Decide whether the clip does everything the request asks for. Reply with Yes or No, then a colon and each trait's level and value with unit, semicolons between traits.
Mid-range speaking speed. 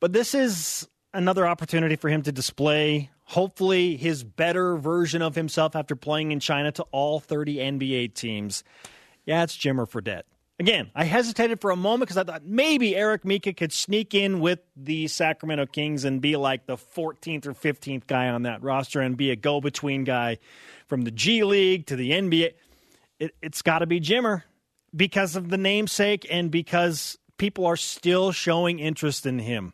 Yes: average, 180 wpm